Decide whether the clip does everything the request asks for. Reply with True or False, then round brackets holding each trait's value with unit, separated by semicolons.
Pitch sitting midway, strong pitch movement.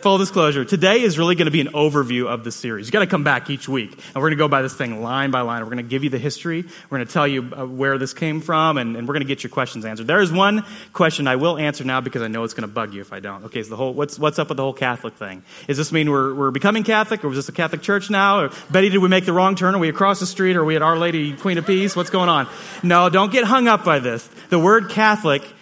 True (150 Hz; 6.0 semitones)